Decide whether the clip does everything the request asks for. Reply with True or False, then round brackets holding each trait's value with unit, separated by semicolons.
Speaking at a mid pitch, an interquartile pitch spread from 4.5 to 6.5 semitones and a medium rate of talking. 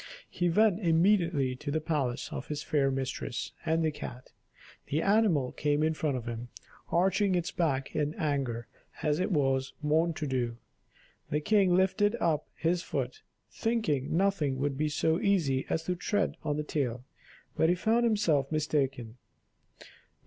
True (155 Hz; 4.8 semitones; 160 wpm)